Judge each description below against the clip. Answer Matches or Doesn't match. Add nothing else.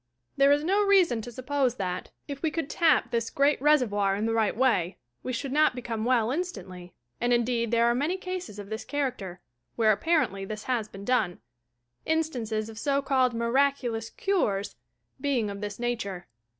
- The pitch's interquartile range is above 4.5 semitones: Matches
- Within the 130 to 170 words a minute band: Doesn't match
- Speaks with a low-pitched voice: Doesn't match